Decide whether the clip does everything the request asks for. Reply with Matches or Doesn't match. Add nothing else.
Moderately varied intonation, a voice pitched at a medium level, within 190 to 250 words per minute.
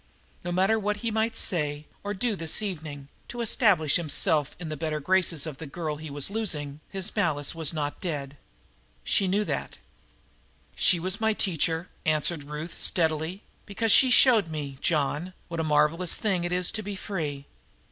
Doesn't match